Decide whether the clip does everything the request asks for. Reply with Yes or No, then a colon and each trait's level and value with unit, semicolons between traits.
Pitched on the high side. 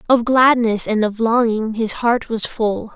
Yes: high, 225 Hz